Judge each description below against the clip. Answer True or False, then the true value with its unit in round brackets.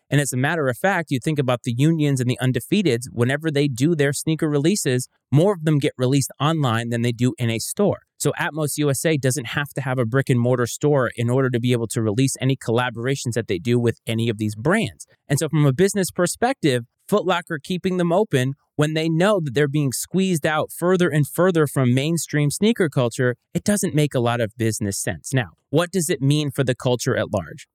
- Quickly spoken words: True (225 wpm)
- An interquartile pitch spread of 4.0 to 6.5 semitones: True (4.3 semitones)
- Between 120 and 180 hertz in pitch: True (140 Hz)